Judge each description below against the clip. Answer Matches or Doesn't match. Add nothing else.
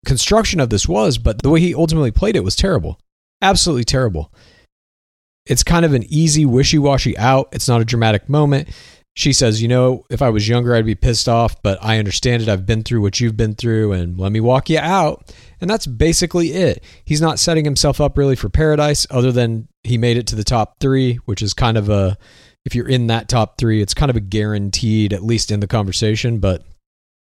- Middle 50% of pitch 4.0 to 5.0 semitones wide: Matches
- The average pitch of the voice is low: Matches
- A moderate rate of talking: Doesn't match